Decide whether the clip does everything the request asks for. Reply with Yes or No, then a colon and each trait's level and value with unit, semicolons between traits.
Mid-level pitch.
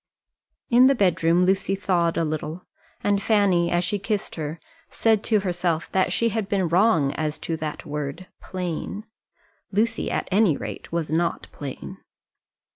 Yes: medium, 180 Hz